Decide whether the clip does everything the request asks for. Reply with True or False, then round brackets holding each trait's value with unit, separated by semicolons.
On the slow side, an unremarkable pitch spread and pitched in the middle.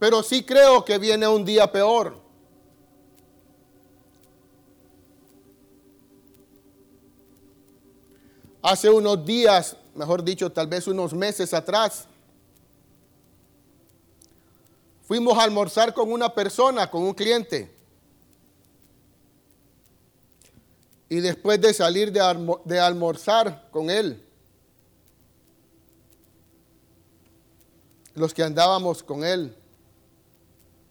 False (80 wpm; 7.6 semitones; 180 Hz)